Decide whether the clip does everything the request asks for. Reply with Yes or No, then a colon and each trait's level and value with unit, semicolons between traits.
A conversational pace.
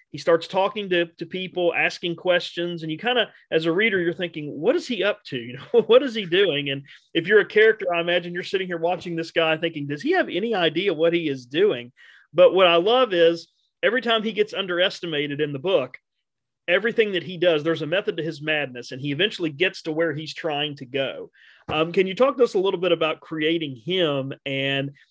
No: fast, 230 wpm